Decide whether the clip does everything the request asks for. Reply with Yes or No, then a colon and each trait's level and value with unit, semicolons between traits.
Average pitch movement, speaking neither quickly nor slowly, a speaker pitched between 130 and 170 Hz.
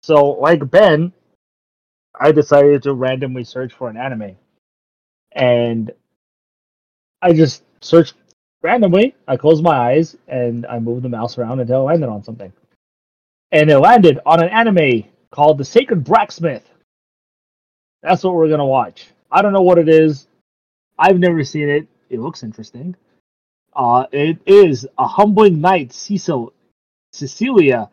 No: wide, 6.0 semitones; average, 145 wpm; medium, 140 Hz